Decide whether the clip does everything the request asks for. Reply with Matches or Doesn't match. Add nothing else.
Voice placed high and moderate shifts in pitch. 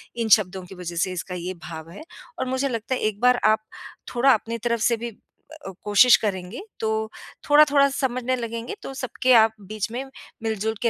Matches